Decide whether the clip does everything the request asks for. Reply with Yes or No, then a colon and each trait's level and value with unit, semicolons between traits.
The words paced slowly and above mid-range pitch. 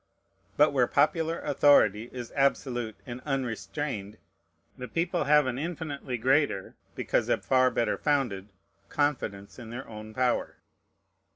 No: slow, 125 wpm; low, 130 Hz